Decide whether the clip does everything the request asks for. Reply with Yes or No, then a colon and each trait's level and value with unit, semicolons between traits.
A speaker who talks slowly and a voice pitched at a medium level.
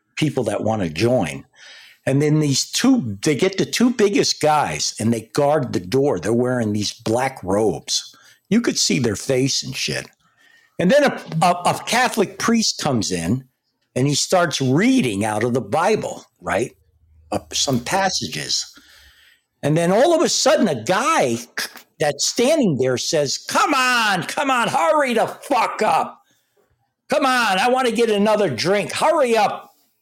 No: average, 165 wpm; medium, 150 Hz